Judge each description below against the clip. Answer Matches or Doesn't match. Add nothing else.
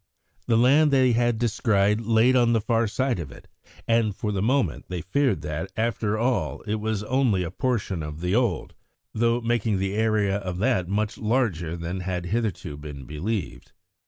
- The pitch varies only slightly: Doesn't match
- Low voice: Matches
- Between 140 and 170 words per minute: Doesn't match